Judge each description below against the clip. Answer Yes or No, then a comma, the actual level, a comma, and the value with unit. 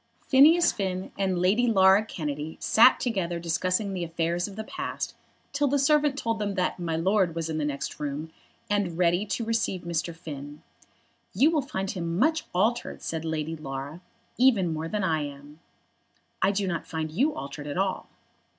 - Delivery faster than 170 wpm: Yes, average, 180 wpm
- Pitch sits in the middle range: Yes, medium, 180 Hz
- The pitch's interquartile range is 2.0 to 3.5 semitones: No, average, 5.0 semitones